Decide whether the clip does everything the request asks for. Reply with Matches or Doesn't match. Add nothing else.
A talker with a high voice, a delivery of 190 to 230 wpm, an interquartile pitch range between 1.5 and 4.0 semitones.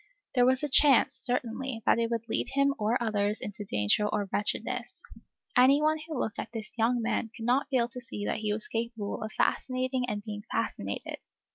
Matches